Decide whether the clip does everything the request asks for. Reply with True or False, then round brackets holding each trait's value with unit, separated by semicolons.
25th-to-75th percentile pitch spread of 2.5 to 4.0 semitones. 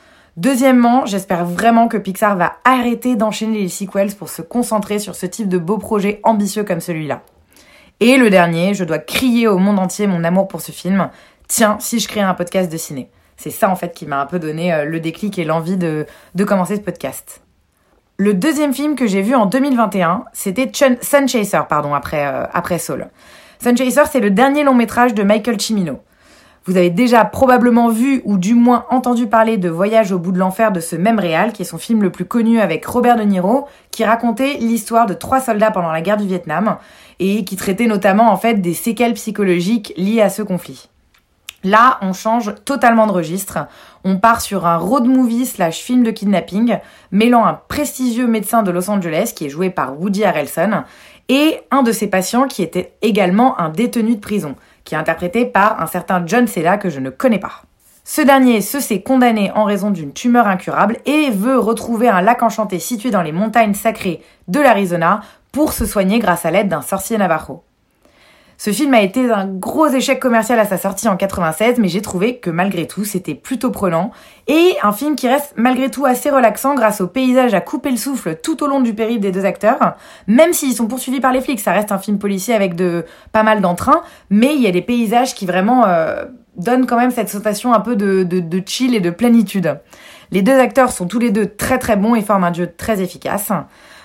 False (4.6 semitones)